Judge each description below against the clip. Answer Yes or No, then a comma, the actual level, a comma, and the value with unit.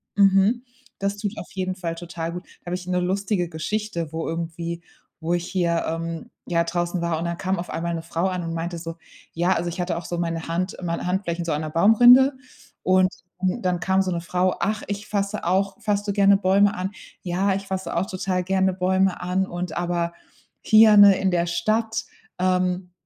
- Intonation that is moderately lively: No, narrow, 2.3 semitones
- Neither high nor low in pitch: Yes, medium, 180 Hz